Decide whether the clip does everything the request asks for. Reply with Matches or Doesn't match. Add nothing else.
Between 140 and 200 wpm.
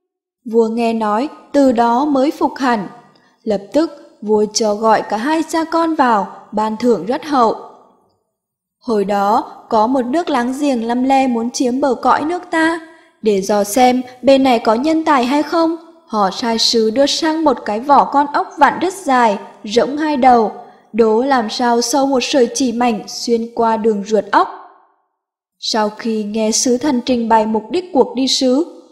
Matches